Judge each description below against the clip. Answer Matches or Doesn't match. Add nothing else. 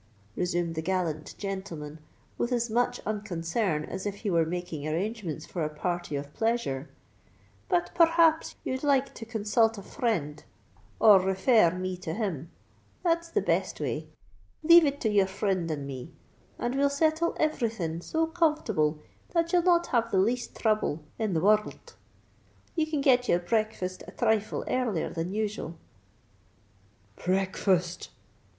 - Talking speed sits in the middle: Matches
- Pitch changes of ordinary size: Doesn't match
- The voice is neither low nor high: Doesn't match